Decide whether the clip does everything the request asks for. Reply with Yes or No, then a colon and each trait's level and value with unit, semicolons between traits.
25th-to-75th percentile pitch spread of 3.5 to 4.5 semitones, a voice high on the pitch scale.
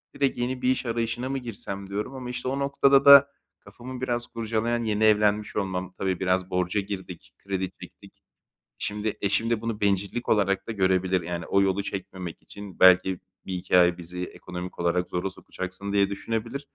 No: average, 4.0 semitones; low, 100 Hz